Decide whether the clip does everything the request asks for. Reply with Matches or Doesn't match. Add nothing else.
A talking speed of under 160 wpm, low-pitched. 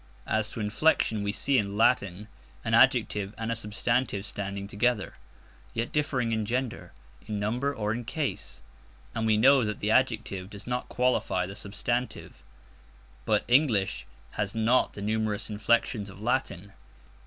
Matches